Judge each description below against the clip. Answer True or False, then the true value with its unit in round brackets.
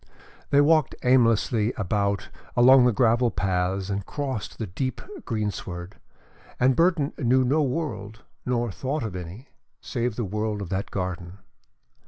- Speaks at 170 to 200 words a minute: False (140 wpm)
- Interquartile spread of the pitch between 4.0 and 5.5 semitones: True (4.5 semitones)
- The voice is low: True (115 Hz)